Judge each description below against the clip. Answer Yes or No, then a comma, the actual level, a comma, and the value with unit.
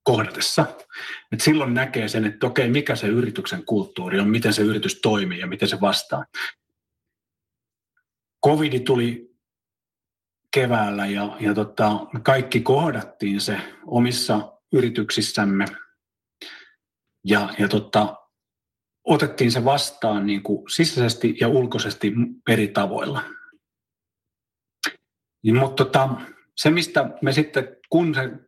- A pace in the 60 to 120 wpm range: Yes, average, 100 wpm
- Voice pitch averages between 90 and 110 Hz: No, low, 125 Hz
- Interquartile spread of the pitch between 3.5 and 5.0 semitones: Yes, average, 4.2 semitones